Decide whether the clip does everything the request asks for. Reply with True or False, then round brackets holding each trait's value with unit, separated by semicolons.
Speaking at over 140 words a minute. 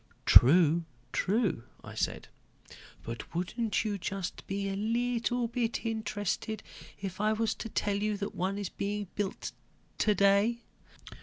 False (135 wpm)